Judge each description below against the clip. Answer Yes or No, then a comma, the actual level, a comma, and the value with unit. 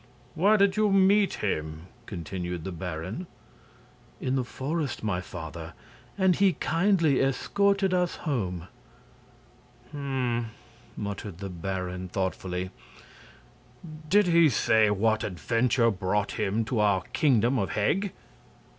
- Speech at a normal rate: No, slow, 115 wpm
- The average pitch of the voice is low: Yes, low, 115 Hz